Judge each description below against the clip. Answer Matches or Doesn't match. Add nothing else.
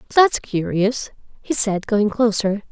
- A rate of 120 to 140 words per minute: Matches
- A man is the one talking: Doesn't match